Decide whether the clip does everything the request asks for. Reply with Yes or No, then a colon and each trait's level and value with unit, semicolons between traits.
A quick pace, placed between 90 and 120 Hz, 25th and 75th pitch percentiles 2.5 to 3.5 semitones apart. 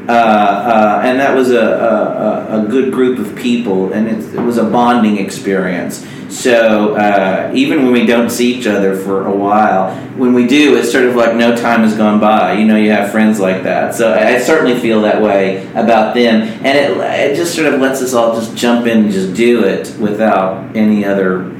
Yes: fast, 215 wpm; low, 110 Hz; average, 2.9 semitones